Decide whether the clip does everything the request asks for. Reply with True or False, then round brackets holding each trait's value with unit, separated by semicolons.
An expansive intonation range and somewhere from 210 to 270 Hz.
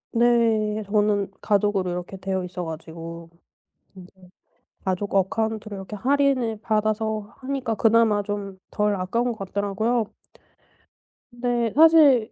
False (3.2 semitones; 215 Hz)